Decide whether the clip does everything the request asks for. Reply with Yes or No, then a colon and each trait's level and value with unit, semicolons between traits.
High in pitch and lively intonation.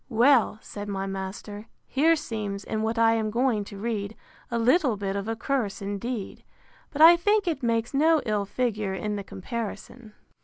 No: high, 225 Hz; average, 3.8 semitones